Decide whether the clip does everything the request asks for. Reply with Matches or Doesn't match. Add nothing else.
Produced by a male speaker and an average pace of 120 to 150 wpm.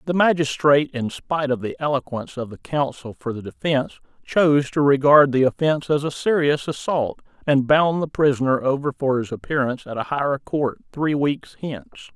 Doesn't match